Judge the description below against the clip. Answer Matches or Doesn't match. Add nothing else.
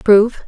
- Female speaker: Matches